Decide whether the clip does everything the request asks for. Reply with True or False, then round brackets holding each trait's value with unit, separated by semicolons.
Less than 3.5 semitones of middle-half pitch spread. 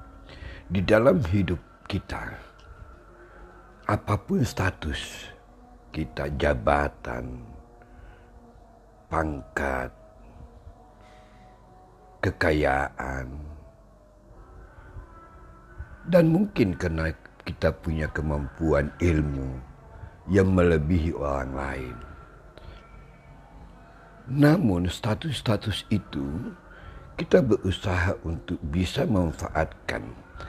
False (4.9 semitones)